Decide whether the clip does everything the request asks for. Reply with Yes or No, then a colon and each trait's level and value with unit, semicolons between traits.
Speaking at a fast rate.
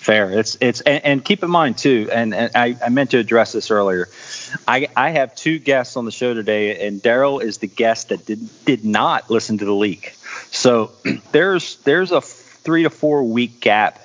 Yes: fast, 210 wpm